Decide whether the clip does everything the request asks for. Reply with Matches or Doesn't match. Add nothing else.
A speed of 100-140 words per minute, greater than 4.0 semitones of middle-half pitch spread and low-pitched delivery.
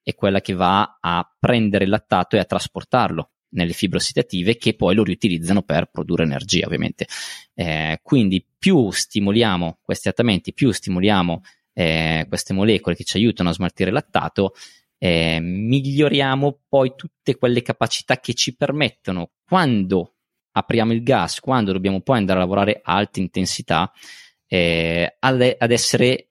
Doesn't match